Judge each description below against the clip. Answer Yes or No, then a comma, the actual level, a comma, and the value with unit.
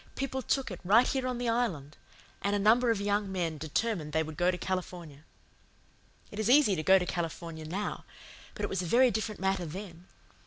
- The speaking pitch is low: No, high, 190 Hz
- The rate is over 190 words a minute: Yes, fast, 205 wpm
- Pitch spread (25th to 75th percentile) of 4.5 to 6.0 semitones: Yes, average, 5.0 semitones